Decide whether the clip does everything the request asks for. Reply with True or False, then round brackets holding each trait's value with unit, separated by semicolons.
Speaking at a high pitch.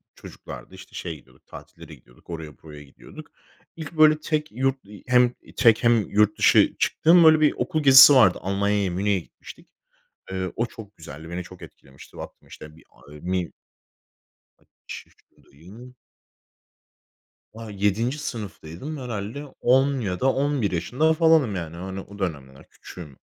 False (105 Hz)